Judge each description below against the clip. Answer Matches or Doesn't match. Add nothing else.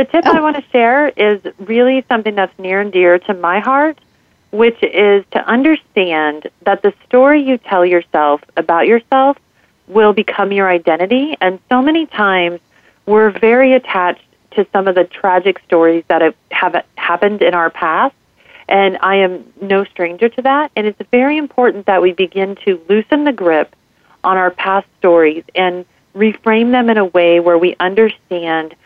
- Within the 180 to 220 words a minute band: Doesn't match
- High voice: Matches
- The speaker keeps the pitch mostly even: Doesn't match